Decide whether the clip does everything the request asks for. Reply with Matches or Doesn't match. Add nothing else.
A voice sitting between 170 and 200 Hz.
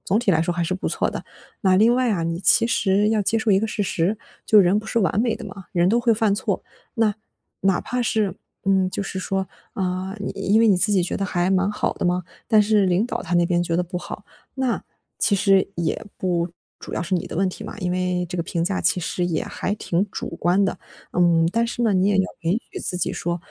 Matches